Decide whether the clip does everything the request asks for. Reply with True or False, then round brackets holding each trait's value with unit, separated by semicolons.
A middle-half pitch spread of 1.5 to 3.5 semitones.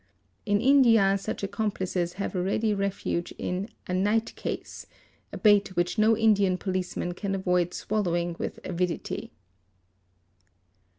True (2.7 semitones)